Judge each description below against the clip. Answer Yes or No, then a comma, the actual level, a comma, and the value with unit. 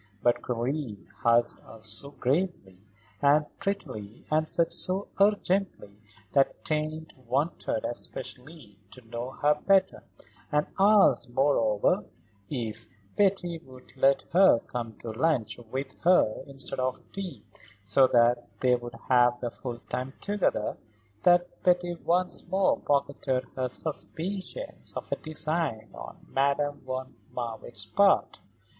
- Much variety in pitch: Yes, wide, 6.0 semitones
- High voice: No, low, 135 Hz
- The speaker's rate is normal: No, slow, 125 wpm